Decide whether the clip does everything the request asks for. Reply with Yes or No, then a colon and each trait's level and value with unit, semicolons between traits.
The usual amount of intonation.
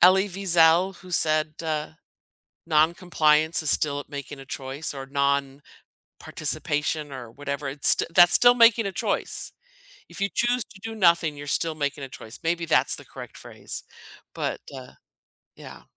Yes: average, 4.0 semitones